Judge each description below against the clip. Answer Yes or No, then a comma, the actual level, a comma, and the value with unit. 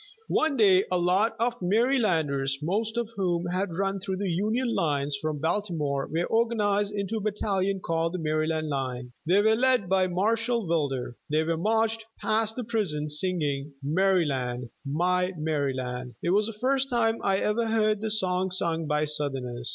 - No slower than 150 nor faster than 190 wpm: Yes, average, 165 wpm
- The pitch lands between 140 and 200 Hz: Yes, medium, 185 Hz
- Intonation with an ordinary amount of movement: No, wide, 6.1 semitones